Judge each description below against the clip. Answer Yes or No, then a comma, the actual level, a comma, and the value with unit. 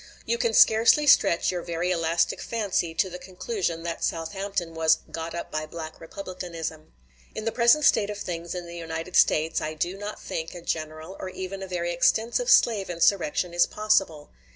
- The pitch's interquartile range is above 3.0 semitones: Yes, average, 3.6 semitones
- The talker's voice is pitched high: No, medium, 175 Hz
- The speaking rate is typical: Yes, average, 180 wpm